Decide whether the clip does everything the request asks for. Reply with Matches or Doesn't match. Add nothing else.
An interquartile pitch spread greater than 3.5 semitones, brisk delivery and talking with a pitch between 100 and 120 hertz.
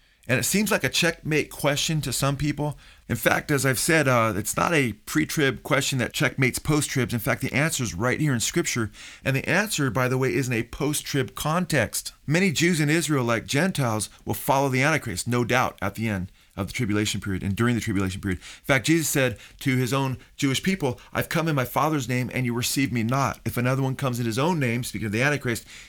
Doesn't match